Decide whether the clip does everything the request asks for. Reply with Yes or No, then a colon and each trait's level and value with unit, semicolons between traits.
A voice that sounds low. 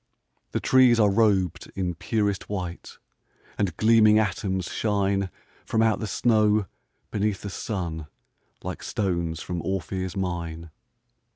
Yes: low, 100 Hz